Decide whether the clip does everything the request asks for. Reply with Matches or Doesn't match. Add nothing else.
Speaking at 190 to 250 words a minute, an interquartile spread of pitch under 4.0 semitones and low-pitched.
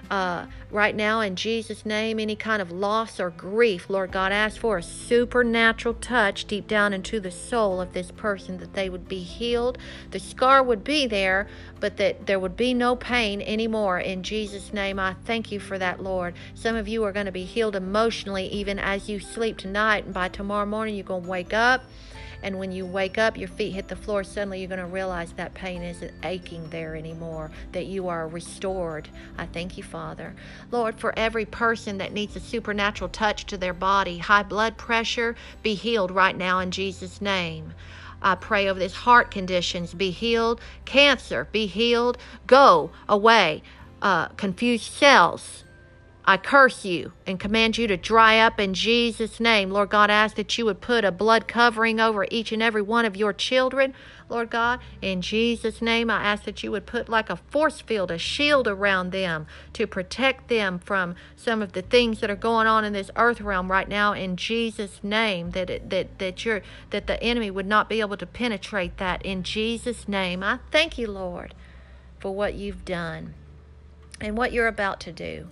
Doesn't match